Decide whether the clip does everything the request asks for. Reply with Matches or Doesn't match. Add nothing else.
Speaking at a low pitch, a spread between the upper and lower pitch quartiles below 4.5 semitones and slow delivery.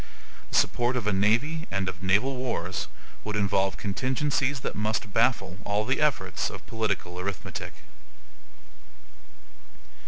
Doesn't match